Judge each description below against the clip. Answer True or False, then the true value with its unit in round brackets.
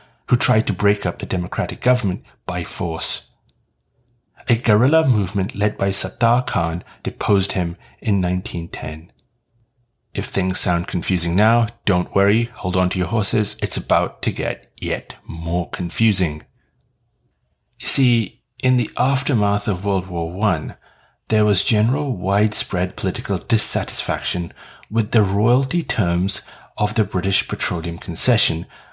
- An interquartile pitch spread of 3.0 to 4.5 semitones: True (4.2 semitones)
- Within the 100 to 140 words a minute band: True (135 wpm)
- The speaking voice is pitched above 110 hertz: False (105 Hz)